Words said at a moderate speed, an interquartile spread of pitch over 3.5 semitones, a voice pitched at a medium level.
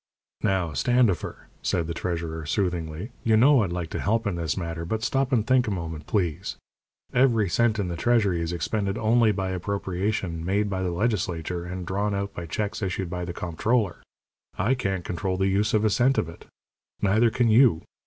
No: average, 195 wpm; average, 4.1 semitones; very low, 95 Hz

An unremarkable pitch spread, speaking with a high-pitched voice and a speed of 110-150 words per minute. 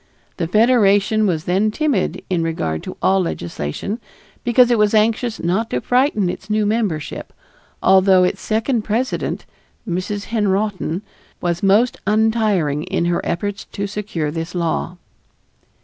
Yes: average, 3.8 semitones; high, 200 Hz; slow, 135 wpm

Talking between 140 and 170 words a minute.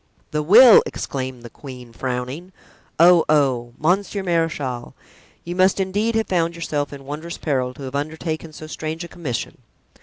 Yes: average, 155 wpm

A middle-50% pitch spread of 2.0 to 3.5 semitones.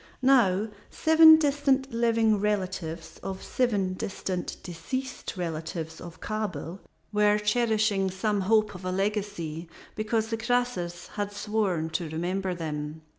No: average, 3.9 semitones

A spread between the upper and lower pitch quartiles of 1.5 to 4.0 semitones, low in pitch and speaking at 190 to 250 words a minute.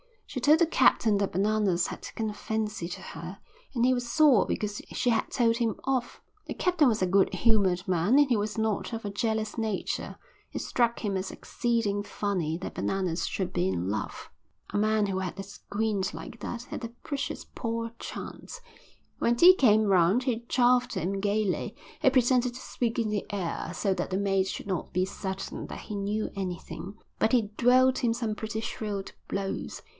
No: average, 3.5 semitones; high, 215 Hz; average, 195 wpm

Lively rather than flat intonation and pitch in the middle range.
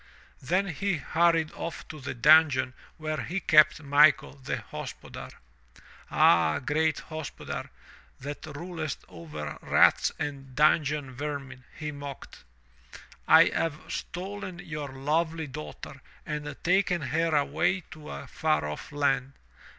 No: average, 3.1 semitones; medium, 150 Hz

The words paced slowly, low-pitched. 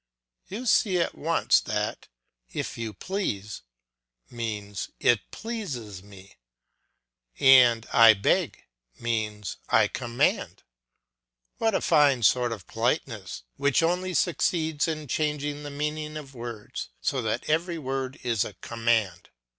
Yes: slow, 125 wpm; low, 130 Hz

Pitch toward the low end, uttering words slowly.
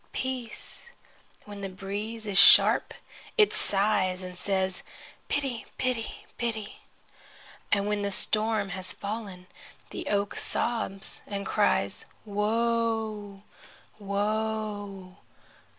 No: high, 205 Hz; slow, 100 wpm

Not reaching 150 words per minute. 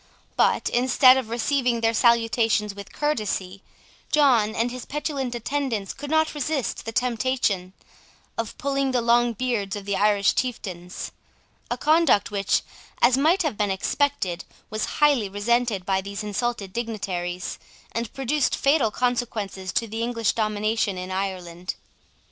Yes: average, 140 wpm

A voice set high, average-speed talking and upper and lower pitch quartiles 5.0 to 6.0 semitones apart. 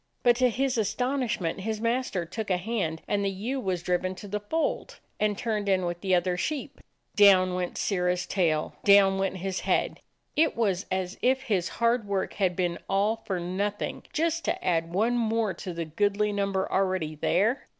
No: high, 200 Hz; average, 185 wpm; average, 3.6 semitones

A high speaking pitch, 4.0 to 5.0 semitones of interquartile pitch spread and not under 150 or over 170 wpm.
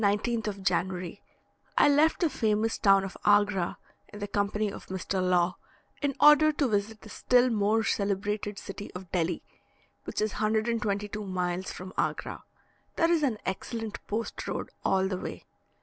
No: high, 205 Hz; average, 2.8 semitones; average, 165 wpm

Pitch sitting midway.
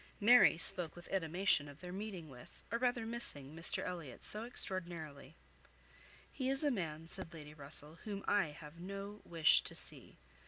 Yes: medium, 175 Hz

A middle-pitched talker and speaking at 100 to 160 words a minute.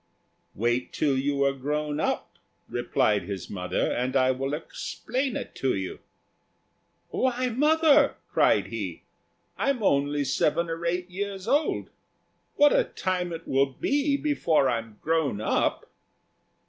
Yes: medium, 150 Hz; slow, 135 wpm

